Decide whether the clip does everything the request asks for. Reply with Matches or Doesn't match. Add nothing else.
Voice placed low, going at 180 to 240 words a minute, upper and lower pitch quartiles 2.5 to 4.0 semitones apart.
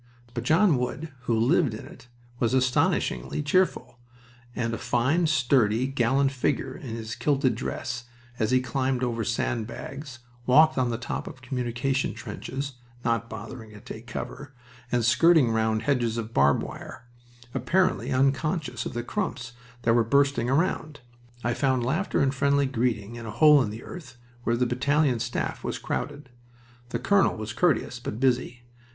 Doesn't match